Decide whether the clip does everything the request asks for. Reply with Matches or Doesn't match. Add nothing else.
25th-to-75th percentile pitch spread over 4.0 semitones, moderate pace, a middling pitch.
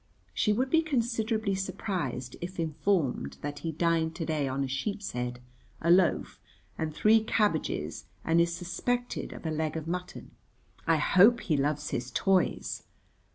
Matches